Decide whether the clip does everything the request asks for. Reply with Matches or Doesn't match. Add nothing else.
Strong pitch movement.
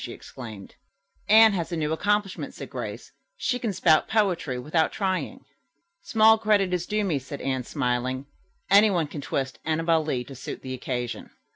Matches